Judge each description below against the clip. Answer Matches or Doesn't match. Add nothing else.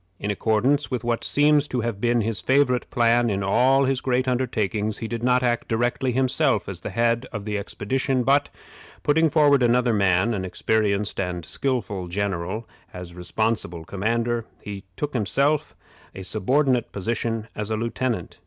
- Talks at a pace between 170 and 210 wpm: Doesn't match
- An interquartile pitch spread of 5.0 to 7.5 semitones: Doesn't match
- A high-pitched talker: Doesn't match